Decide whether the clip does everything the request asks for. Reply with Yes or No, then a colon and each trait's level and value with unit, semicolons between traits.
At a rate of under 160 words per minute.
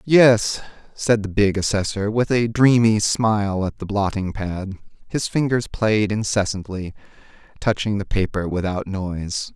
Yes: average, 140 wpm